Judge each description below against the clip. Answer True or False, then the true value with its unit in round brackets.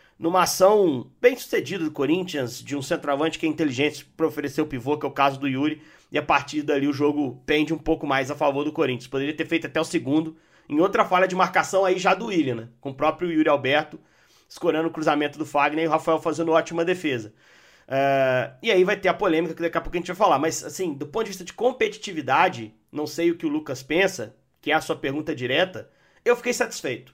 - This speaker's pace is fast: True (235 wpm)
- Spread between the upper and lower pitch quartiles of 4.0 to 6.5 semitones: False (3.4 semitones)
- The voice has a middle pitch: True (160 Hz)